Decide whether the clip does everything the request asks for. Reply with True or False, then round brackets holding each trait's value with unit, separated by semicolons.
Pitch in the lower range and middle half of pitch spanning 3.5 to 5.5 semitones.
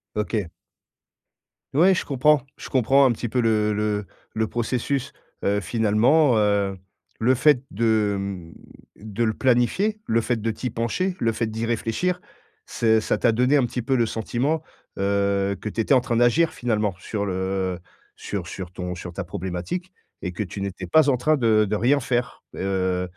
True (110 Hz; 4.1 semitones)